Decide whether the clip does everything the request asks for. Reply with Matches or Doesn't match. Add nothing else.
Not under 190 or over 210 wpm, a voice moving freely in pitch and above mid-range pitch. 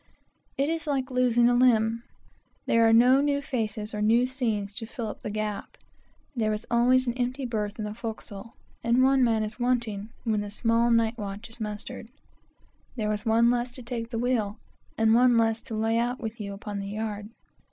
Doesn't match